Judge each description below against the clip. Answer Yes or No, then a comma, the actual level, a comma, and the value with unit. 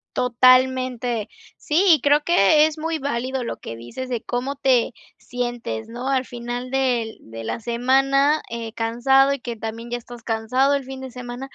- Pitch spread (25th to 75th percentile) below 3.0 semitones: Yes, narrow, 2.4 semitones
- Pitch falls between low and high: No, very high, 250 Hz